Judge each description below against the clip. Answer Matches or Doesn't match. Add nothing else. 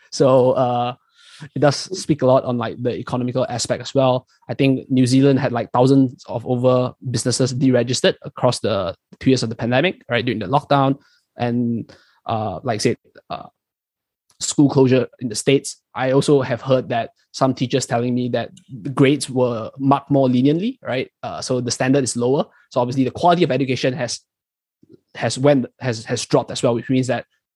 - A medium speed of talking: Matches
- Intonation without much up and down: Matches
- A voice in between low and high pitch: Doesn't match